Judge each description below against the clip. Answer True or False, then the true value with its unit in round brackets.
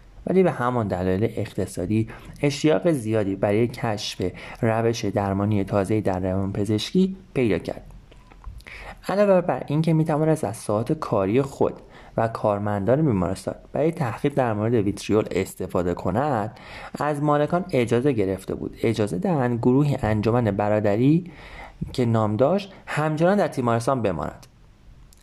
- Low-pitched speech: True (115 Hz)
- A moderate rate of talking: True (125 wpm)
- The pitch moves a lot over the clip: True (6.2 semitones)